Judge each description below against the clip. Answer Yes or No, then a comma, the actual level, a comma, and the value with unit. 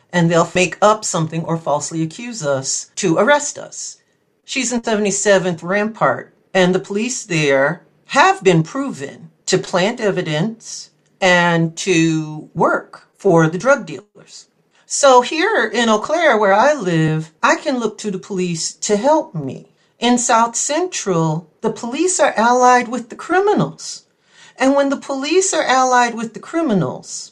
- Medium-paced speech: Yes, average, 150 wpm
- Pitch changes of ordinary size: No, wide, 6.9 semitones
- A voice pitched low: No, high, 205 Hz